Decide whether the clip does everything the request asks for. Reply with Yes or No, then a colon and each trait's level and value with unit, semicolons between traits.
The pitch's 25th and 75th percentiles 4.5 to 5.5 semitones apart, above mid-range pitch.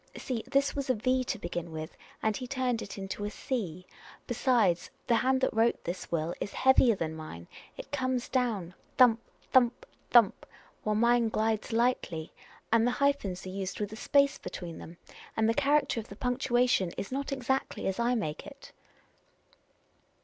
Yes: average, 5.2 semitones; high, 230 Hz